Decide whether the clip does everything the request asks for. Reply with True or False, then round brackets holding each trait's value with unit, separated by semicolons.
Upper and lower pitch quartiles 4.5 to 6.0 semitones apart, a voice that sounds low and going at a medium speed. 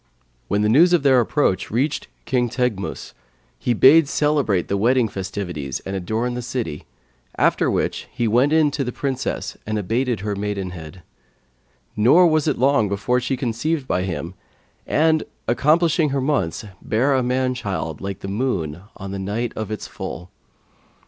True (5.5 semitones; 120 Hz; 160 wpm)